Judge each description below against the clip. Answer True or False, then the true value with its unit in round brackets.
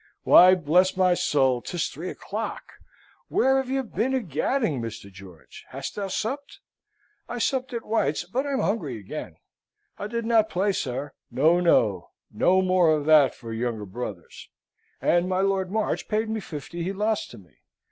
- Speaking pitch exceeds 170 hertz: True (185 Hz)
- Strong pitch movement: True (8.2 semitones)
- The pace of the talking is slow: False (170 wpm)